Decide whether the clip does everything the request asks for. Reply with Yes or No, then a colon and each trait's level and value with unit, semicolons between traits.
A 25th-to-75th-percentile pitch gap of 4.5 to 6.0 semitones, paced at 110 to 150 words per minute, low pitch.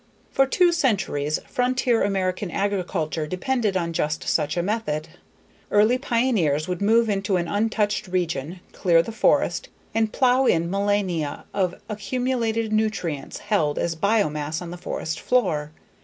No: average, 5.2 semitones; average, 140 wpm; high, 195 Hz